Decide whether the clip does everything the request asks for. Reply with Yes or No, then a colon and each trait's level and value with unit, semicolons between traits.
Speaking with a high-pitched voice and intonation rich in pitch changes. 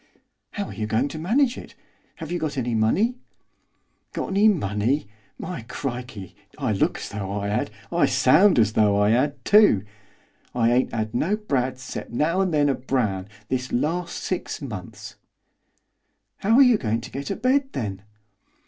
No: low, 130 Hz; wide, 8.7 semitones